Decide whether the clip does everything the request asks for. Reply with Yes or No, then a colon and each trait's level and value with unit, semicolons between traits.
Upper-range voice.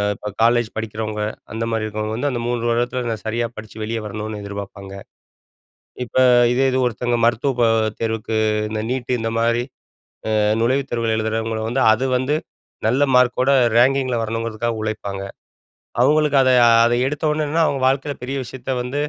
No: low, 115 Hz